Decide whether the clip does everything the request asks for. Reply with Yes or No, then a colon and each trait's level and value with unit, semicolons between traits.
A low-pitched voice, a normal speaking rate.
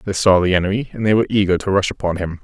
No: very low, 95 Hz; fast, 295 wpm